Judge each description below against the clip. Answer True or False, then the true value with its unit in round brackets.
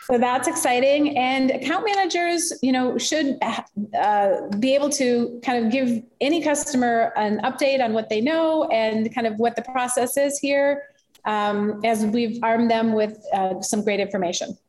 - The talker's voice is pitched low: False (245 Hz)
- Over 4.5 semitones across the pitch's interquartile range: False (4.0 semitones)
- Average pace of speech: True (170 wpm)